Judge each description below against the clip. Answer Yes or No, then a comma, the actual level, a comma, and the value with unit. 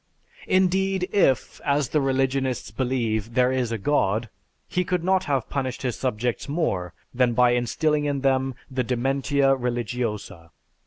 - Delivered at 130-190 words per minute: Yes, average, 145 wpm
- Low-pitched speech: Yes, low, 130 Hz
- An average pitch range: Yes, average, 3.1 semitones